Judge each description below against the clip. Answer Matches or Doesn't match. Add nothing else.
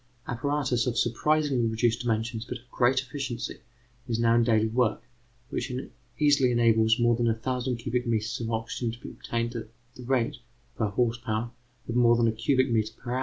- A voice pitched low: Matches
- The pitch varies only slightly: Matches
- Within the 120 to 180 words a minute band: Doesn't match